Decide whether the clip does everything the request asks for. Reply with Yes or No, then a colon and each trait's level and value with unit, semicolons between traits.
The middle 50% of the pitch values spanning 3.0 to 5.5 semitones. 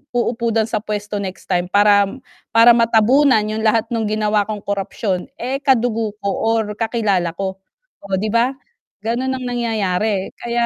No: narrow, 2.5 semitones